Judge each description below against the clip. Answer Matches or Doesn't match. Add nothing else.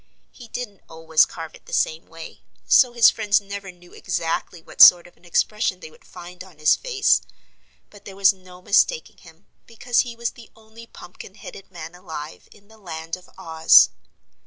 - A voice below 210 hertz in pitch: Matches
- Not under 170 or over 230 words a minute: Matches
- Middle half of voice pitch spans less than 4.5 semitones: Doesn't match